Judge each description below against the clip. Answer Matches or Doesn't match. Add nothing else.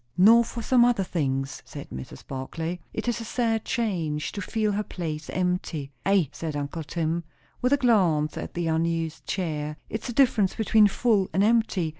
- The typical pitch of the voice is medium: Matches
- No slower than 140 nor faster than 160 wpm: Doesn't match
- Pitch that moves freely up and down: Matches